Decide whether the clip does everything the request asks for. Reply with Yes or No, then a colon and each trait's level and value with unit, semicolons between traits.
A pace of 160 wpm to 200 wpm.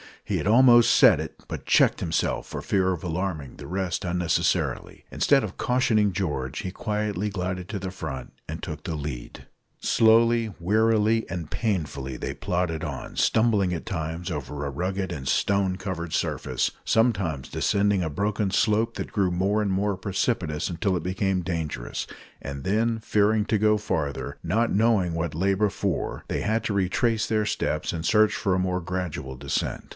Yes: average, 170 wpm